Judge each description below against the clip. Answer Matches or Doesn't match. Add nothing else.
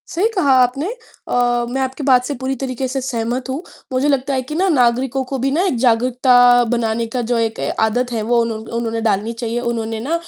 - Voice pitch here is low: Doesn't match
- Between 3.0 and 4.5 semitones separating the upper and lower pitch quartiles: Doesn't match